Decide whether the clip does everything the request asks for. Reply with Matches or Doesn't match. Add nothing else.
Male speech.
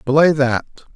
Matches